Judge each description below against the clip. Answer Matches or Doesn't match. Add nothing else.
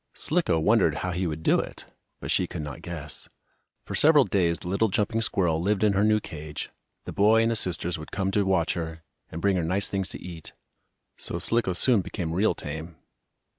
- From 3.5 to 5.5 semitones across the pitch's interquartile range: Matches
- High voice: Doesn't match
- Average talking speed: Doesn't match